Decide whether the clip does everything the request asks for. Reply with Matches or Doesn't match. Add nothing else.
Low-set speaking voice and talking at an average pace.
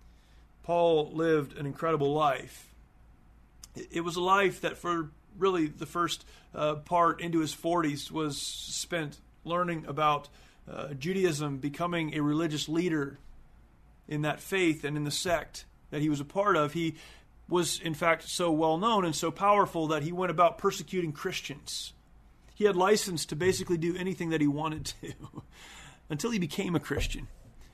Doesn't match